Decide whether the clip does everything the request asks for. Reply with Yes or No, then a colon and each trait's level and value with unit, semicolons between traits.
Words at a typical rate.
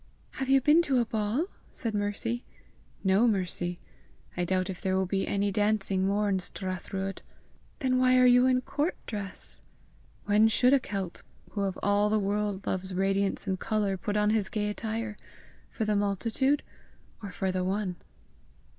Yes: average, 170 wpm